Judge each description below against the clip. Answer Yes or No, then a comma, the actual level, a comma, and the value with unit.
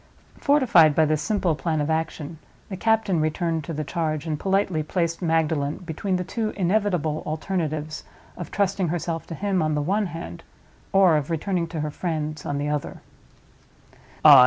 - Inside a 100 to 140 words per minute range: No, average, 165 wpm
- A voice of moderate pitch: Yes, medium, 165 Hz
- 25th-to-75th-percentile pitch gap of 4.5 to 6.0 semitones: No, average, 3.4 semitones